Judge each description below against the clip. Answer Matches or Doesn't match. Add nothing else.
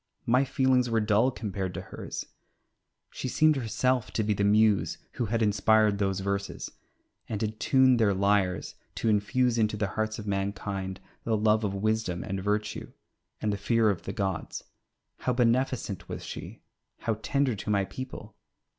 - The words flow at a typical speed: Matches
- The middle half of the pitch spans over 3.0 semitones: Doesn't match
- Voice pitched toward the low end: Matches